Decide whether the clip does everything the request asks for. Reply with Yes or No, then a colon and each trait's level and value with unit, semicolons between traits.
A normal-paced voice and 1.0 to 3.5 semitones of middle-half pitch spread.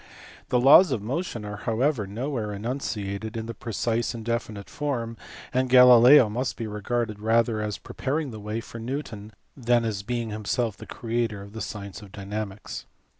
Yes: average, 170 wpm; average, 2.7 semitones